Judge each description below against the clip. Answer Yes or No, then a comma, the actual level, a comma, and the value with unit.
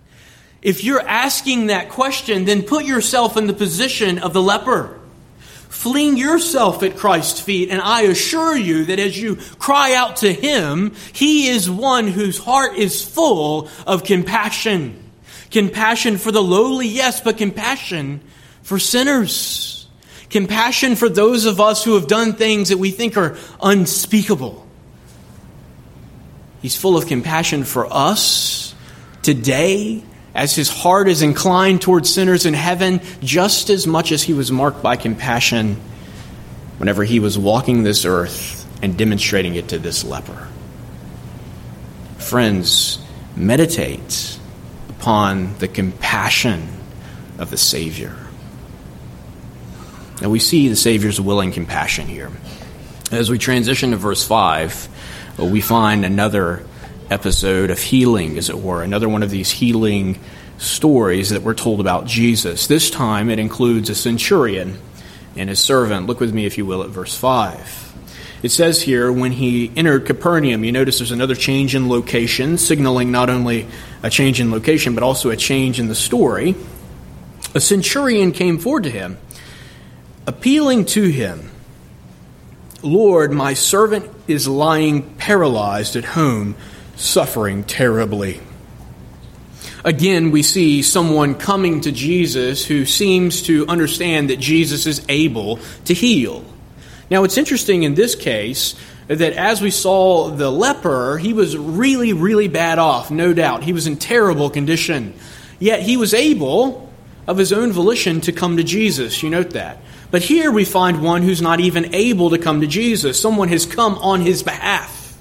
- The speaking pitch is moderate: Yes, medium, 160 Hz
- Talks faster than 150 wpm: No, average, 145 wpm